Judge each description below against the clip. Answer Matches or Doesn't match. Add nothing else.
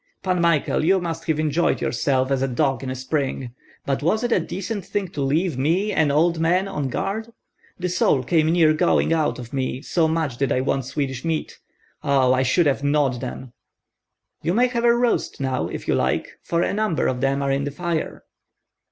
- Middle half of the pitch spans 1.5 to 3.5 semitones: Doesn't match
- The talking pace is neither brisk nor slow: Doesn't match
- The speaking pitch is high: Doesn't match